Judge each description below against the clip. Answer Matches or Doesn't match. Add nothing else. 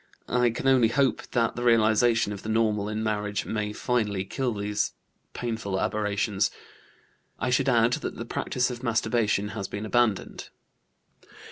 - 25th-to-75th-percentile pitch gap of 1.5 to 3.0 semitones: Matches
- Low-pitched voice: Matches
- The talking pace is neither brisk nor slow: Matches